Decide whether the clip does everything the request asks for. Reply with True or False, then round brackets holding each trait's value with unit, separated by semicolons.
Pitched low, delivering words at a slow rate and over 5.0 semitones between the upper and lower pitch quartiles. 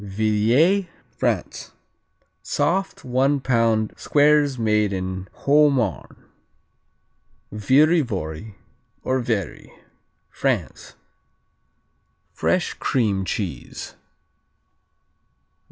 True (115 Hz; 70 wpm; 5.6 semitones)